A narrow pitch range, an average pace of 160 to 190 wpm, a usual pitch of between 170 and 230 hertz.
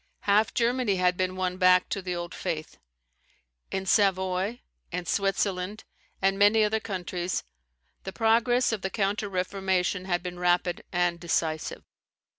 No: narrow, 2.1 semitones; average, 140 wpm; high, 190 Hz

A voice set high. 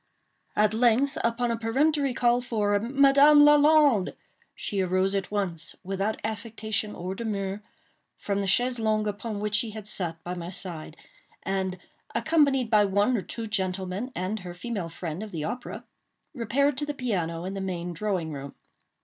Yes: high, 210 Hz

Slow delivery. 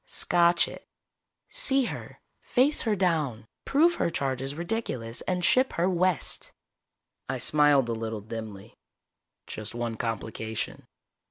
Yes: slow, 125 wpm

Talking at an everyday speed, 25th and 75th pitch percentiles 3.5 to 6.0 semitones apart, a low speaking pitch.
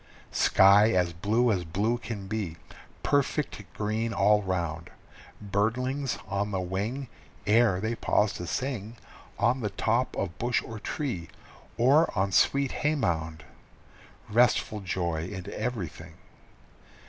No: slow, 125 wpm; average, 4.4 semitones; low, 105 Hz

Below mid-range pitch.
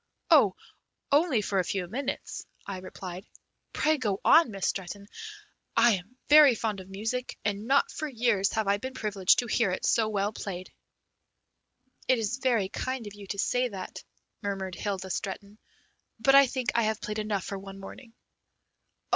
No: high, 210 Hz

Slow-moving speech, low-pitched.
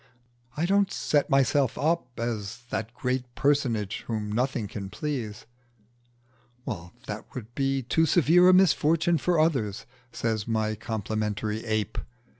Yes: slow, 125 wpm; low, 120 Hz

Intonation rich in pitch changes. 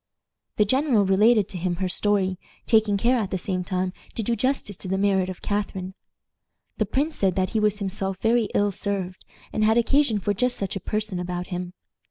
No: average, 2.8 semitones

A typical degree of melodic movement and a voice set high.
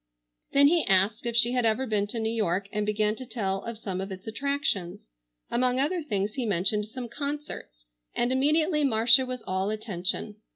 Yes: average, 4.3 semitones; high, 225 Hz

